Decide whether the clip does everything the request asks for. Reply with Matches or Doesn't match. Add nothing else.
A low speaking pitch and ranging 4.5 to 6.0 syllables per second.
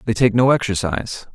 Matches